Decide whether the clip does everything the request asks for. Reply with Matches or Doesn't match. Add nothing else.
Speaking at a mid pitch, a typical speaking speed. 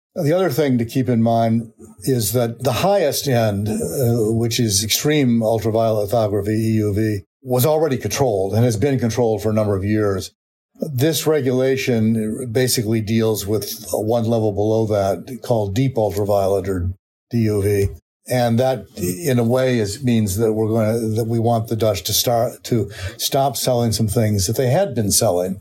Doesn't match